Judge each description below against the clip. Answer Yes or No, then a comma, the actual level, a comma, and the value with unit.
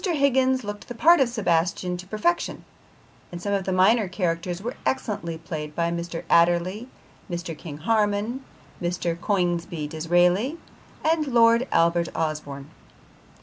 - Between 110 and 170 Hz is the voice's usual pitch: No, medium, 185 Hz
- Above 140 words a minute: No, slow, 135 wpm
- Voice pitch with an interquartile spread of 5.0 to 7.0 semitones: Yes, wide, 5.4 semitones